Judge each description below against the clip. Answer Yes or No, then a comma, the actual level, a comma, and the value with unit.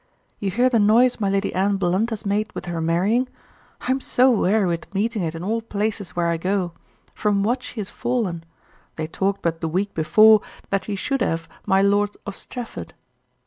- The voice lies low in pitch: No, high, 200 Hz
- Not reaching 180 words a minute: No, average, 200 wpm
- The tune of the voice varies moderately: Yes, average, 3.7 semitones